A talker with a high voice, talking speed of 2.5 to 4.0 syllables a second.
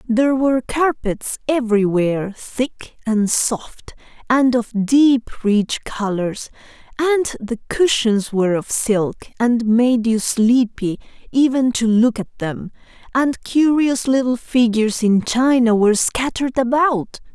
Yes: high, 240 Hz; 3.9 syllables/s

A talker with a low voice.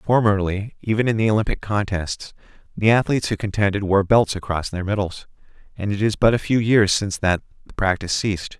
Yes: low, 100 Hz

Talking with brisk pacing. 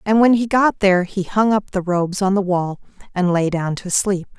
Yes: fast, 245 wpm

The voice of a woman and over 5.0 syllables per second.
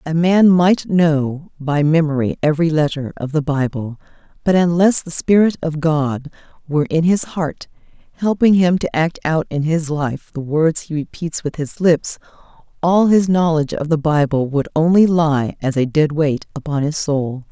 No: female; 4.5 syllables/s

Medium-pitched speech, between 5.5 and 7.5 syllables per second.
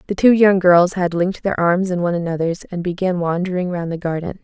Yes: medium, 180 Hz; 5.9 syllables/s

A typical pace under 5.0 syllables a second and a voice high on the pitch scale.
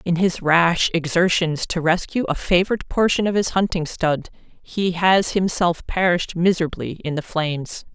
No: 4.7 syllables/s; medium, 175 Hz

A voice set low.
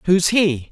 No: medium, 175 Hz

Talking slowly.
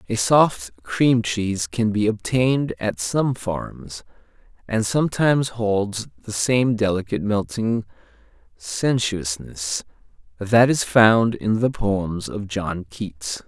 Yes: slow, 120 wpm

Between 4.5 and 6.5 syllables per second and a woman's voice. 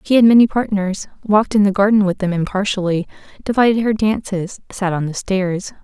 Yes: 5.5 syllables/s; female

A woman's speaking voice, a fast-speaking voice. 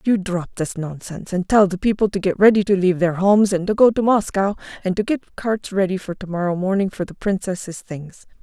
Yes: female; fast, 220 wpm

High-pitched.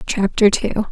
Yes: high, 205 Hz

